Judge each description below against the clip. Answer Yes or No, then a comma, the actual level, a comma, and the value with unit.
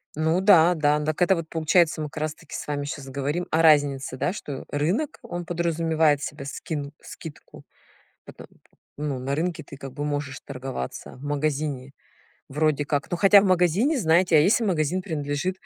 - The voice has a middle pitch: Yes, medium, 155 Hz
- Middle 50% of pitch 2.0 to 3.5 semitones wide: Yes, average, 3.1 semitones